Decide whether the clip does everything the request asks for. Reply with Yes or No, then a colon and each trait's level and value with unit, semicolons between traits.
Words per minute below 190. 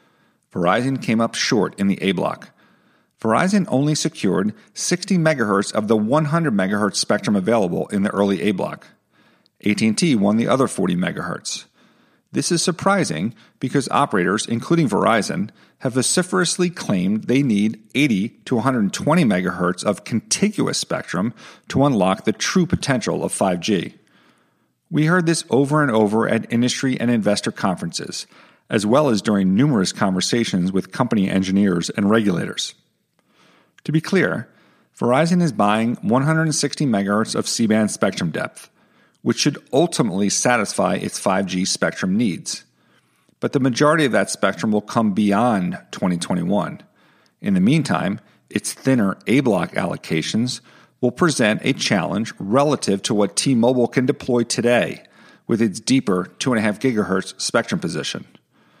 Yes: average, 140 wpm